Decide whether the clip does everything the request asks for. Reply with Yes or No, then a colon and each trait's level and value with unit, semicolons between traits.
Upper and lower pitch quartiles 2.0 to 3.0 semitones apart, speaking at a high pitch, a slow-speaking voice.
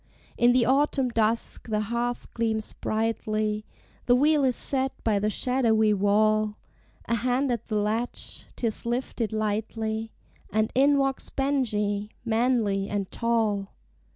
Yes: narrow, 2.5 semitones; high, 225 Hz; slow, 130 wpm